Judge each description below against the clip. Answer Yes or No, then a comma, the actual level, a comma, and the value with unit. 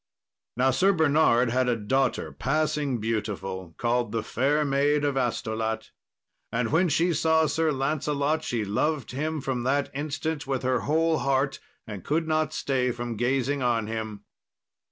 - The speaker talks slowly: No, average, 155 wpm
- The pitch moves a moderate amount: Yes, average, 4.4 semitones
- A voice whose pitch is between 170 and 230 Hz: No, low, 135 Hz